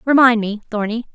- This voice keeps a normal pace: Yes, average, 155 wpm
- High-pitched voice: Yes, high, 230 Hz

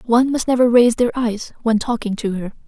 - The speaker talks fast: Yes, fast, 225 wpm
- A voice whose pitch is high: Yes, high, 235 Hz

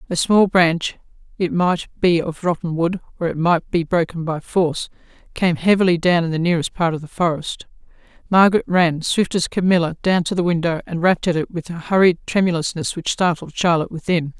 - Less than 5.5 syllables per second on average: No, 5.6 syllables/s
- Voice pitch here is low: No, medium, 170 Hz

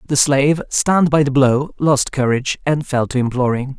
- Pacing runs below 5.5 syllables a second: Yes, 5.3 syllables/s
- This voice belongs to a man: Yes, male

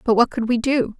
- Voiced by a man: No, female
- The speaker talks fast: Yes, fast, 300 wpm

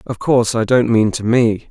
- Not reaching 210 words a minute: No, fast, 245 wpm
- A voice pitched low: Yes, low, 115 Hz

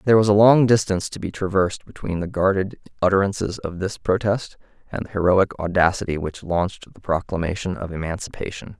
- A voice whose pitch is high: No, very low, 95 Hz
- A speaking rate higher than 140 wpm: Yes, average, 170 wpm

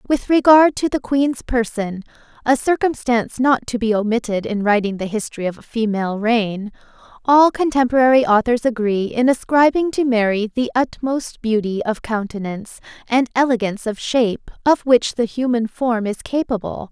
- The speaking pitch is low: No, high, 235 Hz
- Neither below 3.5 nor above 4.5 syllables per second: No, 5.1 syllables/s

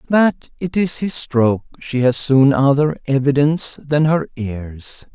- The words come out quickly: No, average, 150 wpm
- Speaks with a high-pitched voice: No, medium, 140 Hz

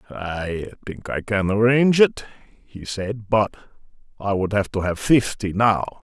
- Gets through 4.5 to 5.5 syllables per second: No, 4.2 syllables/s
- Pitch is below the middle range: Yes, low, 105 Hz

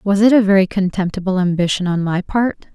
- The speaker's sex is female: Yes, female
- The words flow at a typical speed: Yes, average, 195 wpm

